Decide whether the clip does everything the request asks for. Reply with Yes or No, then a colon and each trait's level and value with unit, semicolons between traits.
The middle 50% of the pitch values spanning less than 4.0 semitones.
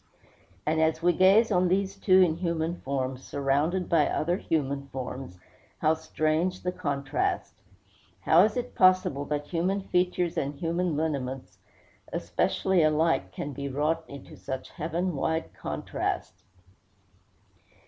No: average, 4.3 semitones